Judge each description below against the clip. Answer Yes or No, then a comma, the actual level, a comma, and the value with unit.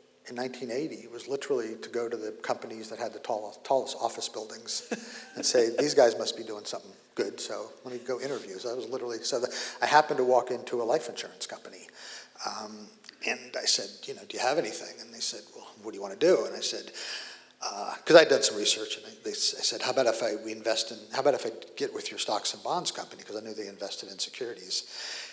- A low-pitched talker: Yes, low, 130 Hz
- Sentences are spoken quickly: Yes, fast, 240 wpm